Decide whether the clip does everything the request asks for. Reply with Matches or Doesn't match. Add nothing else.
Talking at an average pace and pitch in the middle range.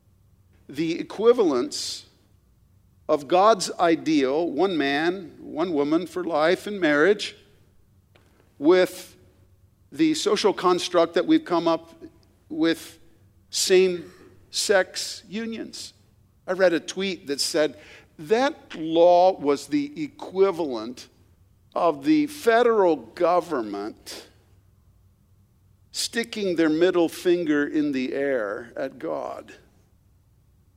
Doesn't match